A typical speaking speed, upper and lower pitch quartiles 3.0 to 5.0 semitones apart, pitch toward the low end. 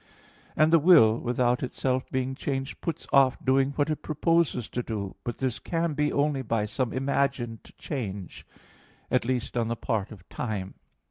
Yes: average, 165 wpm; average, 3.7 semitones; low, 130 Hz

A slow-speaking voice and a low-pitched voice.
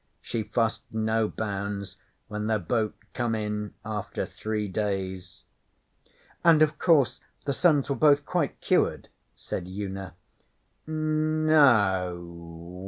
Yes: slow, 115 wpm; low, 110 Hz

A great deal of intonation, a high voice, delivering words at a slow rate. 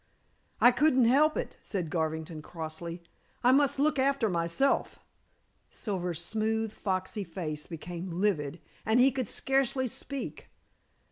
Yes: wide, 7.5 semitones; high, 200 Hz; slow, 125 wpm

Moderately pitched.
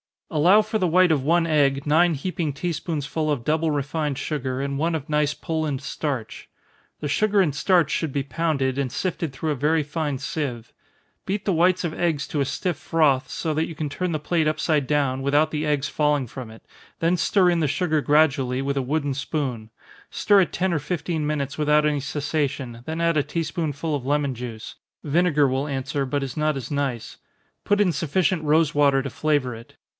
Yes: medium, 150 Hz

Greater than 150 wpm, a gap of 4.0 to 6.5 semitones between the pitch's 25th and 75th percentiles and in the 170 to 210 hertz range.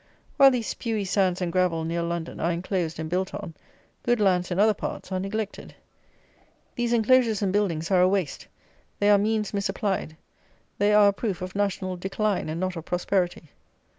No: average, 180 wpm; average, 2.9 semitones; high, 190 Hz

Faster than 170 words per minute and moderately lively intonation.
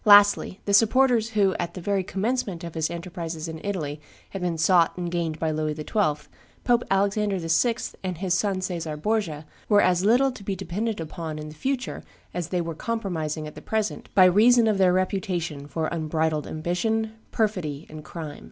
Yes: average, 185 wpm; average, 4.4 semitones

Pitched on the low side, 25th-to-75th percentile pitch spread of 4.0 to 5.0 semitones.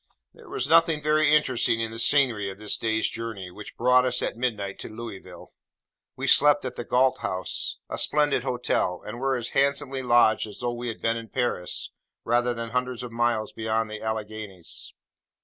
No: low, 120 Hz; average, 2.8 semitones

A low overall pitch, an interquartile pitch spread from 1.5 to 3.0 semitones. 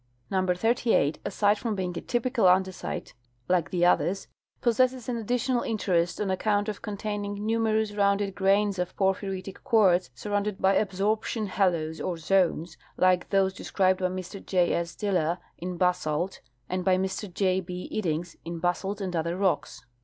No: high, 190 Hz; narrow, 2.6 semitones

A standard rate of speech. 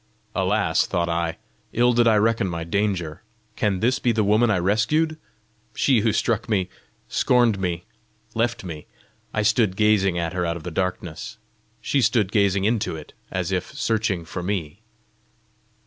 Yes: average, 165 wpm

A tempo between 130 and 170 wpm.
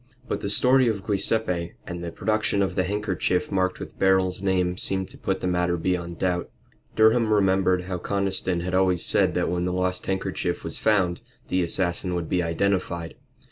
No: average, 180 wpm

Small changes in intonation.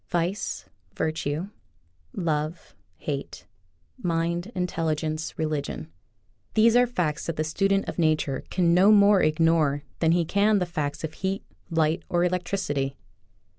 No: average, 3.2 semitones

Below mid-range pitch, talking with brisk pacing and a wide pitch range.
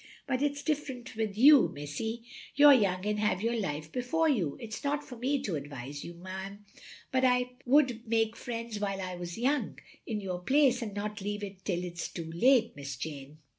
No: high, 215 Hz; fast, 210 wpm; wide, 6.0 semitones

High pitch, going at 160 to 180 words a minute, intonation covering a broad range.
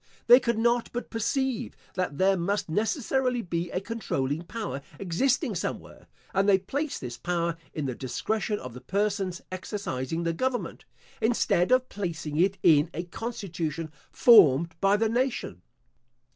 No: high, 195 Hz; average, 145 wpm; wide, 5.7 semitones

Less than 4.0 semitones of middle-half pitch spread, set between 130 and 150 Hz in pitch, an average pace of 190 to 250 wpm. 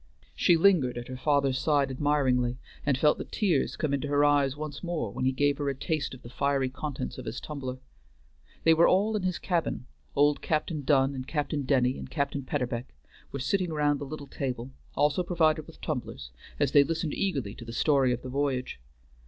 Yes: average, 2.9 semitones; medium, 140 Hz; average, 200 wpm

